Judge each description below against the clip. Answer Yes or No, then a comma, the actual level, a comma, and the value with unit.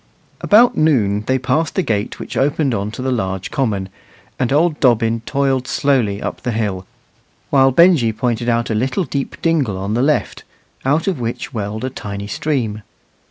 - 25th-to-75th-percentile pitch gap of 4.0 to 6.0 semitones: Yes, average, 4.7 semitones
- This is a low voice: Yes, low, 125 Hz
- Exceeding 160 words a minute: Yes, average, 175 wpm